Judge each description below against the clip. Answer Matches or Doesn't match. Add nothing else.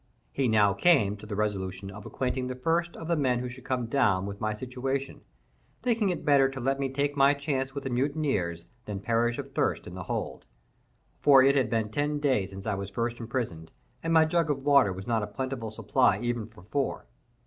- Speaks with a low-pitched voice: Matches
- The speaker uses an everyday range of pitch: Matches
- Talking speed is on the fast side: Matches